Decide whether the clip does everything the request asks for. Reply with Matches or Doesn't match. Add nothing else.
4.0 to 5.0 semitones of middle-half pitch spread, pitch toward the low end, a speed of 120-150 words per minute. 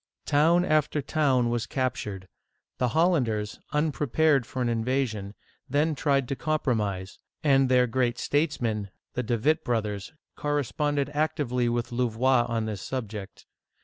Matches